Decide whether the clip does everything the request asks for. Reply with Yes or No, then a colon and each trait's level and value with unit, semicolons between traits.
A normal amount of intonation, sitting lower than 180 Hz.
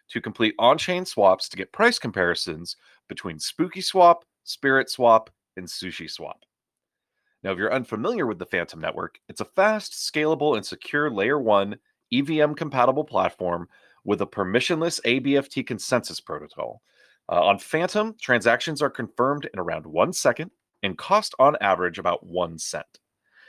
No: wide, 6.8 semitones; low, 135 Hz